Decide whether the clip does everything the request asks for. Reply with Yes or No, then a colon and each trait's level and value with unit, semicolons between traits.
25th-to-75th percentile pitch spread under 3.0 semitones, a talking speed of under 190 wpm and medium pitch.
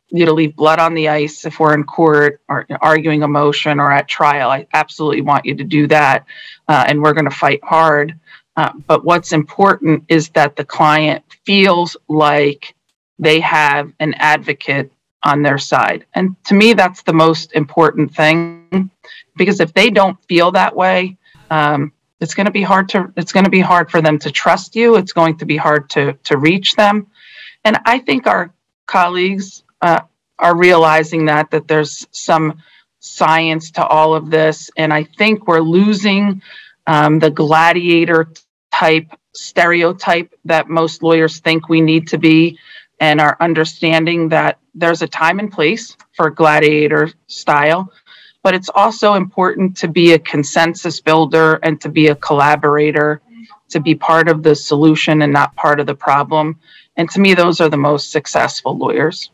Yes: narrow, 2.4 semitones; average, 175 wpm; medium, 160 Hz